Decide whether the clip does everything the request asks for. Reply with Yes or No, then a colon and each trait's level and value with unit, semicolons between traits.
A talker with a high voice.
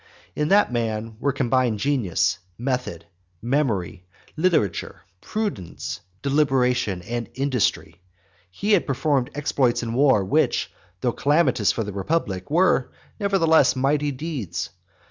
No: low, 130 Hz